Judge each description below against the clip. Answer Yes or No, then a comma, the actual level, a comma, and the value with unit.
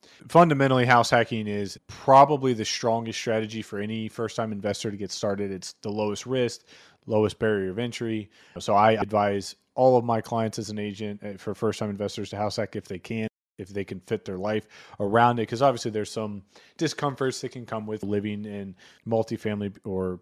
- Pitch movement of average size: No, narrow, 2.3 semitones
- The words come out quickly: No, average, 195 wpm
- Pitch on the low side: Yes, low, 110 Hz